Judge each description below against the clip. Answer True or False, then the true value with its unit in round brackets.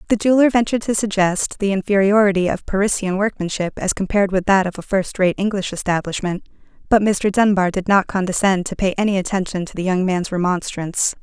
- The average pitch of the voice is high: True (195 Hz)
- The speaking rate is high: False (185 wpm)